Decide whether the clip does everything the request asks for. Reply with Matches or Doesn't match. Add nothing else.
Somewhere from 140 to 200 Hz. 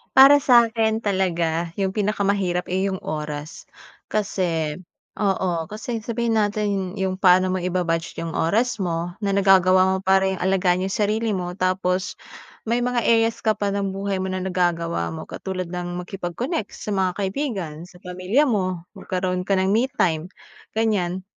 Matches